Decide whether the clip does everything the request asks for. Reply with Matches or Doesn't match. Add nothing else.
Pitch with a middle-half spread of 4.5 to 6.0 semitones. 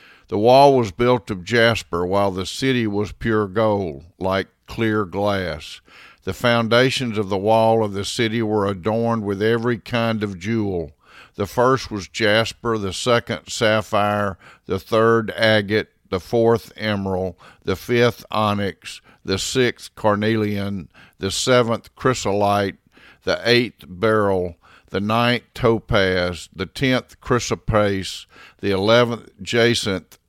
Doesn't match